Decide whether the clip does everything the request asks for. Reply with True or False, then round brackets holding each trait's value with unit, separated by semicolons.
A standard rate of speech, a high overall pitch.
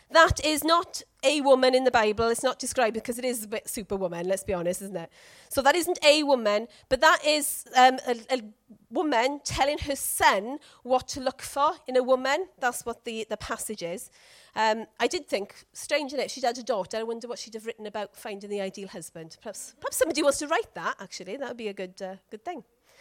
False (230 wpm; 245 Hz)